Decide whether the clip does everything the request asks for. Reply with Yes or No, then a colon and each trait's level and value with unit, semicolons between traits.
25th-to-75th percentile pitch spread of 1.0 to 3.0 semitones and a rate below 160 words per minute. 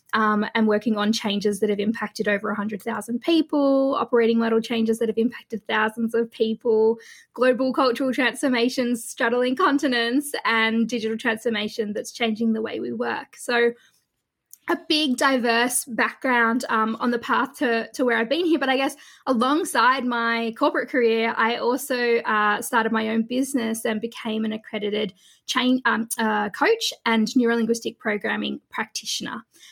Yes: narrow, 2.4 semitones; average, 150 wpm